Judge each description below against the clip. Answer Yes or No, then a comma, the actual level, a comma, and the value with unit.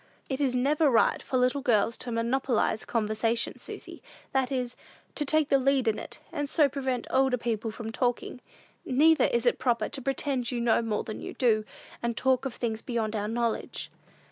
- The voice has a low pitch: No, very high, 250 Hz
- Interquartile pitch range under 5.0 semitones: Yes, average, 2.8 semitones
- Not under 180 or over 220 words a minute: Yes, average, 190 wpm